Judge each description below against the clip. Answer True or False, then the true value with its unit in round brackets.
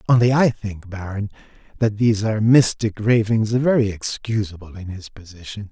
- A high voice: False (105 Hz)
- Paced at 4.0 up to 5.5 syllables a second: True (5.2 syllables/s)